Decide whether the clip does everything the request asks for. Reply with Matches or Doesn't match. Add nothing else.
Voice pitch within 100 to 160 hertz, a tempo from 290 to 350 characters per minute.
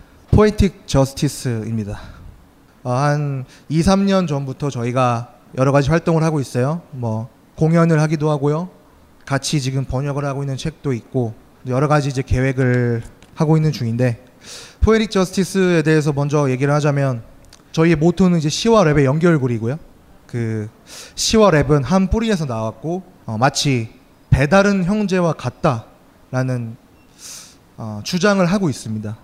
Matches